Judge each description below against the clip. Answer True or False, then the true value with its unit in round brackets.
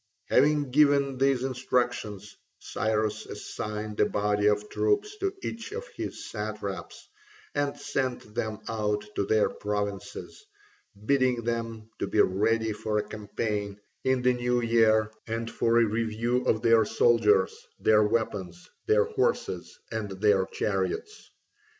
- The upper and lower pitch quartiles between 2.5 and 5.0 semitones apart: True (3.3 semitones)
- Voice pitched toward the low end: True (110 Hz)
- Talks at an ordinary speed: False (130 wpm)